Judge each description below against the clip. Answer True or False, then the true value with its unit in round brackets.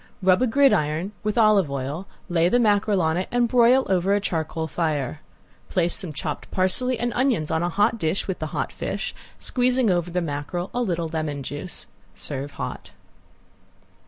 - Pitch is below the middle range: False (180 Hz)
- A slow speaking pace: False (175 wpm)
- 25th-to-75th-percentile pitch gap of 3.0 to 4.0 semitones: False (5.6 semitones)